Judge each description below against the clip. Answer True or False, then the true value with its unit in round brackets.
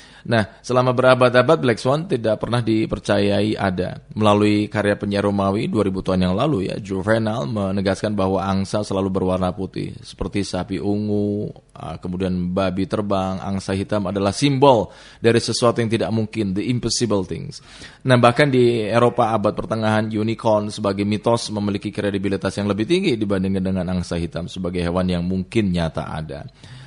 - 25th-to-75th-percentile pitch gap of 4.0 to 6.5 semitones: False (2.8 semitones)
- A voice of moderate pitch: False (105 Hz)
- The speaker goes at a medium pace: False (145 wpm)